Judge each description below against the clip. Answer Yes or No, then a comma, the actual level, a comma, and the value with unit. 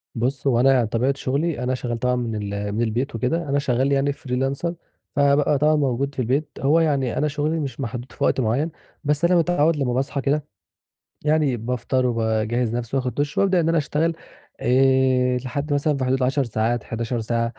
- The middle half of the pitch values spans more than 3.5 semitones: No, average, 3.2 semitones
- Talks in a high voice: No, low, 130 Hz